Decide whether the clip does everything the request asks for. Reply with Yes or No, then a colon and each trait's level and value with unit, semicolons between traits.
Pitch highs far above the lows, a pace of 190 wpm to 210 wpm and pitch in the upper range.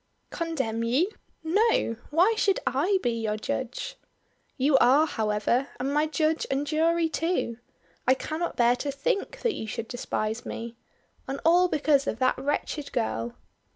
No: wide, 5.7 semitones; average, 155 wpm; very high, 280 Hz